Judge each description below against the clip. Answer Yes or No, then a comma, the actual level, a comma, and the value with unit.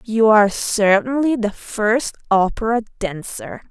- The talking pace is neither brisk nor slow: No, slow, 115 wpm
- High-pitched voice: Yes, high, 220 Hz